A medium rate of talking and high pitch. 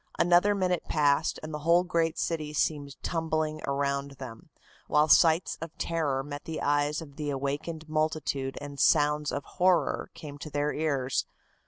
No: average, 160 wpm; medium, 150 Hz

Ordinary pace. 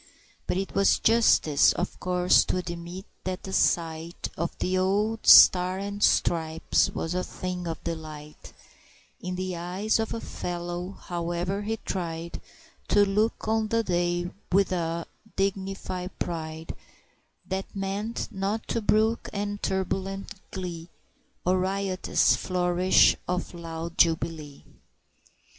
No: slow, 125 wpm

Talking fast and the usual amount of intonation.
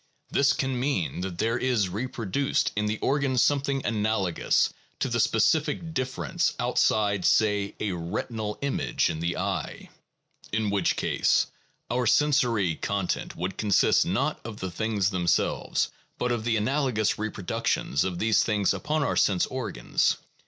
No: average, 145 wpm; average, 4.7 semitones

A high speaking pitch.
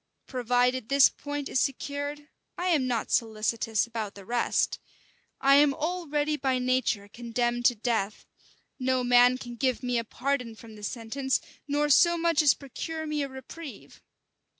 Yes: very high, 255 Hz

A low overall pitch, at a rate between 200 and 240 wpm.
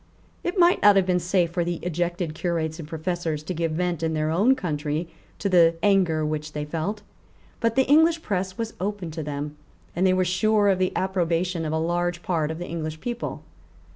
No: medium, 175 Hz; fast, 205 wpm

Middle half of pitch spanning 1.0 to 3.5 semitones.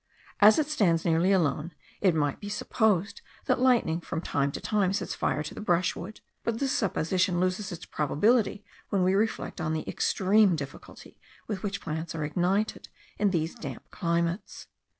No: average, 4.1 semitones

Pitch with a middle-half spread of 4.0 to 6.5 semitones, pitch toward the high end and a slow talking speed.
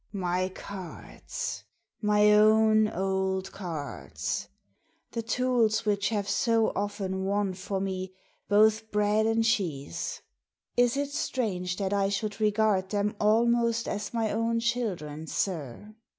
No: average, 2.7 semitones; high, 205 Hz; slow, 130 wpm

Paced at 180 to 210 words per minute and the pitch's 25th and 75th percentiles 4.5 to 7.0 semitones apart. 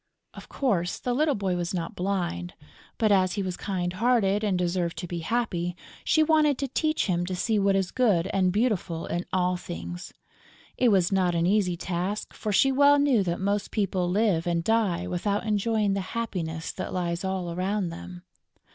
No: average, 190 wpm; average, 3.5 semitones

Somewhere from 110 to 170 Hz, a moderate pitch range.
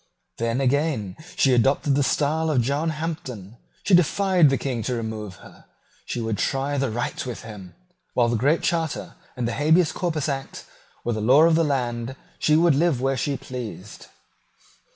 Yes: low, 135 Hz; average, 4.7 semitones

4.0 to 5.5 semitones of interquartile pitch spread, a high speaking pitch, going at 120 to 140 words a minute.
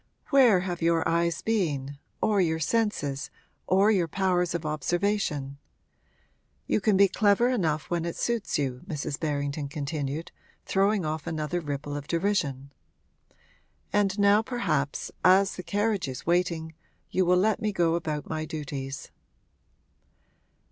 No: average, 5.0 semitones; medium, 170 Hz; slow, 135 wpm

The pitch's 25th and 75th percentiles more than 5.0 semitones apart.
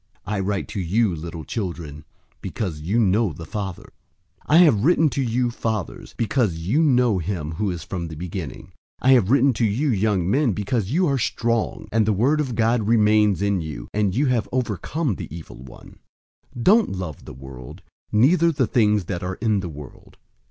Yes: wide, 5.5 semitones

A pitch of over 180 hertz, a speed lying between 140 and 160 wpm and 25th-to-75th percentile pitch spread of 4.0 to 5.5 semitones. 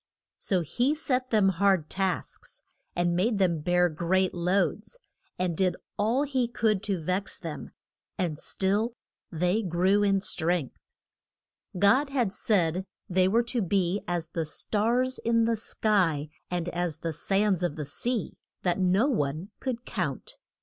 Yes: high, 190 Hz; average, 150 wpm; average, 4.3 semitones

